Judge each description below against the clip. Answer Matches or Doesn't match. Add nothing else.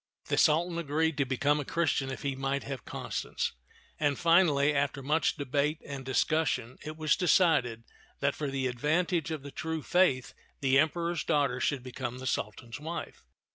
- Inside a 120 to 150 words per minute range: Doesn't match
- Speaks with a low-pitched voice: Doesn't match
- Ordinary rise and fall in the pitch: Matches